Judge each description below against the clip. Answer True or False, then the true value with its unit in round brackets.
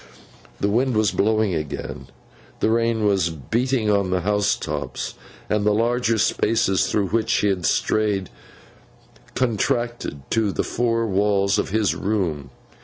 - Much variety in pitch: False (2.8 semitones)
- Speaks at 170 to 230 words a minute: False (140 wpm)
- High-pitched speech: False (105 Hz)